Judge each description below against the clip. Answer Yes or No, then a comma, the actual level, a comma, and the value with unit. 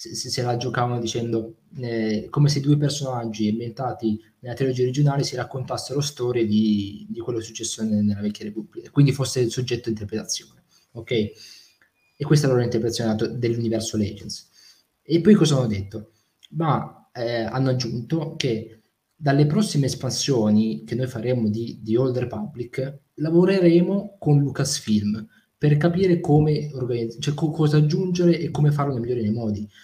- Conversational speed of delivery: Yes, average, 155 wpm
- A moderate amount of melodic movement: Yes, average, 4.5 semitones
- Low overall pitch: Yes, low, 125 Hz